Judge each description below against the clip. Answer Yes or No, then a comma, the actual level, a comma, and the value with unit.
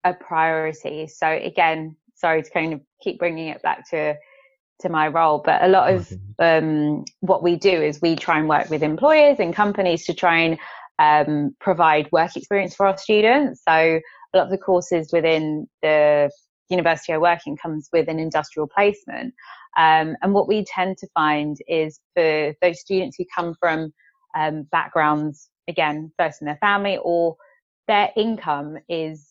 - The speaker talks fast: No, average, 175 wpm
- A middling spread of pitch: Yes, average, 3.1 semitones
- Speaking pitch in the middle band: Yes, medium, 165 Hz